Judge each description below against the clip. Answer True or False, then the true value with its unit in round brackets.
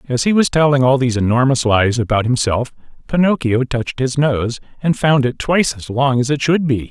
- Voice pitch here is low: True (130 Hz)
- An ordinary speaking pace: False (210 wpm)